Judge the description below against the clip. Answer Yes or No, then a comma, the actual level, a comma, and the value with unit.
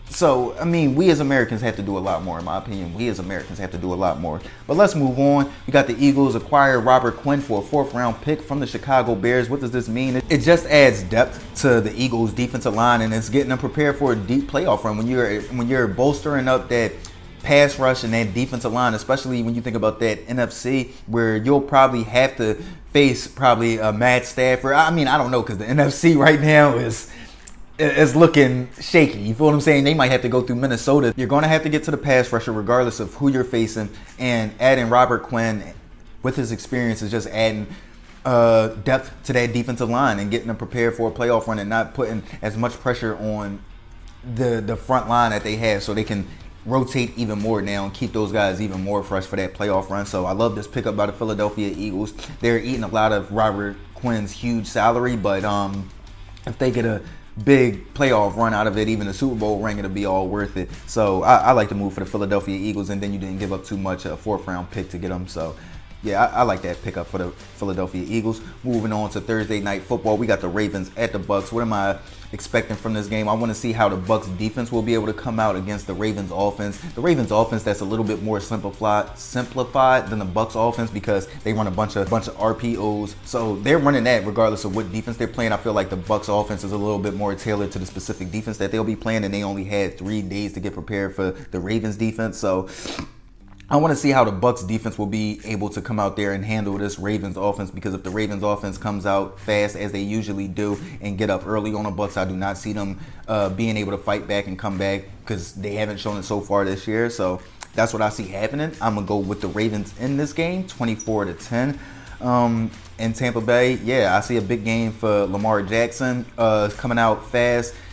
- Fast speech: Yes, fast, 240 wpm